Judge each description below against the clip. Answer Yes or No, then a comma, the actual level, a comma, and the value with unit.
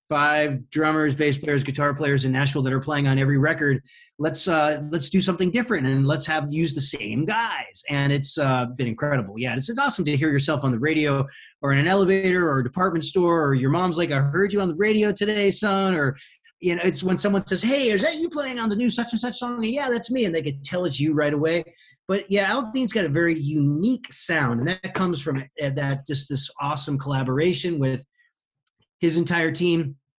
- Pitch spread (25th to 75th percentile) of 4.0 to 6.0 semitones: Yes, average, 5.2 semitones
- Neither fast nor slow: No, fast, 225 wpm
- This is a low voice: No, medium, 155 Hz